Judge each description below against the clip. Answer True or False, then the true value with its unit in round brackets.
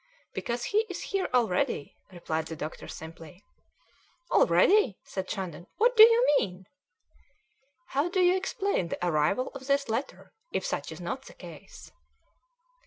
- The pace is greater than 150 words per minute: False (145 wpm)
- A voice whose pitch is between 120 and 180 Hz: False (245 Hz)